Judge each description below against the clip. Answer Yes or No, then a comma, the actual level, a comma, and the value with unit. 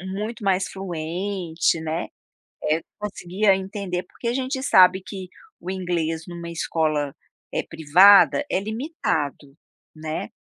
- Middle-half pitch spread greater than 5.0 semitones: No, average, 3.8 semitones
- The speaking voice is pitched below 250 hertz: Yes, medium, 185 Hz